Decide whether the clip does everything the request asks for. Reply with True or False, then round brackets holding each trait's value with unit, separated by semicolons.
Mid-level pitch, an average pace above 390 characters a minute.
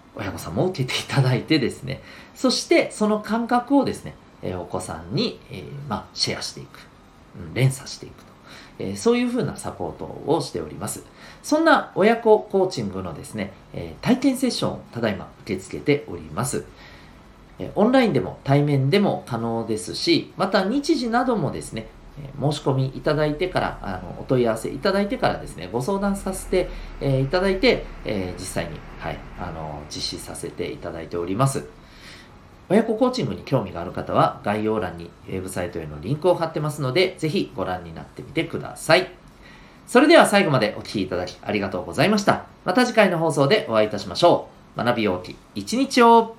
False (145 Hz; 380 characters per minute)